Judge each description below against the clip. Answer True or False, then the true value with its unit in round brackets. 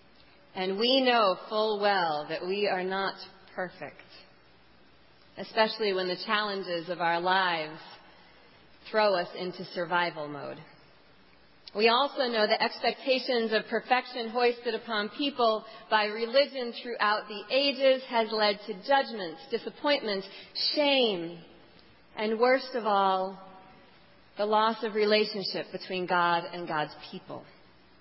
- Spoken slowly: True (120 wpm)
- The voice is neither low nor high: False (210 Hz)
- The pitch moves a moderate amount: True (3.8 semitones)